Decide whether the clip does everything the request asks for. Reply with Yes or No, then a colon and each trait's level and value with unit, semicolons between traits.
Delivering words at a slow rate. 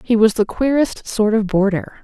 No: fast, 205 wpm